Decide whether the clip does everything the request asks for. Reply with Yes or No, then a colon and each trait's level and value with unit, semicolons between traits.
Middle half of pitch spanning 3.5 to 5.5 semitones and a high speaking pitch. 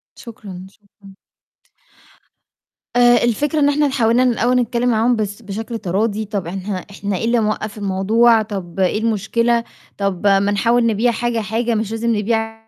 No: average, 2.7 semitones; high, 220 Hz